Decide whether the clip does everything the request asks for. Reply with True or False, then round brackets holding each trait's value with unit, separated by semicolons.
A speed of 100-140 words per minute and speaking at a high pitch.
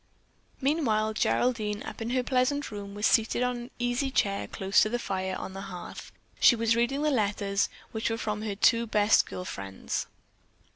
False (185 wpm; 220 Hz)